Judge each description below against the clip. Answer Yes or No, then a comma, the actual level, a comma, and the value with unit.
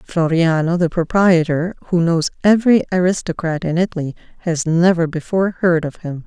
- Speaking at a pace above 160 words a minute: No, average, 145 wpm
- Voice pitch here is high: No, medium, 170 Hz